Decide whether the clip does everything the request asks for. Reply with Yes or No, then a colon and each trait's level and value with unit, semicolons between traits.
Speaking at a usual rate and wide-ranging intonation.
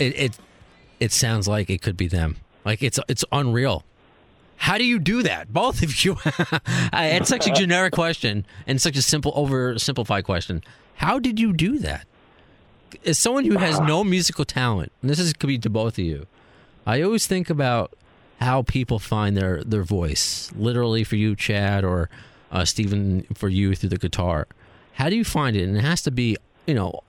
Yes: average, 195 wpm; wide, 7.2 semitones